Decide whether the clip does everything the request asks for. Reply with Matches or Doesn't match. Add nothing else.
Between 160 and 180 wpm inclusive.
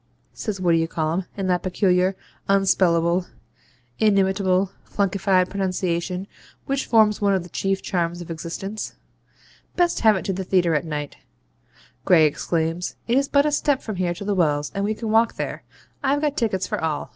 Matches